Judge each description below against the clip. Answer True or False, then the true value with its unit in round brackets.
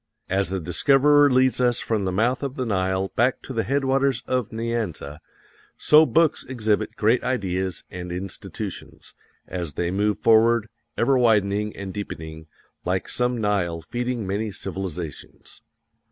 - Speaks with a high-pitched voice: False (105 Hz)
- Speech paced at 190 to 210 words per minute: False (140 wpm)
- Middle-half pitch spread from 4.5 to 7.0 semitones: True (5.0 semitones)